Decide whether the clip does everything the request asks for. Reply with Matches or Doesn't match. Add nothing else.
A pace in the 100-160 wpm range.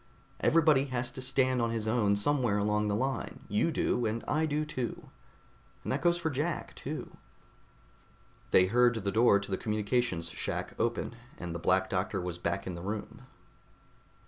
Doesn't match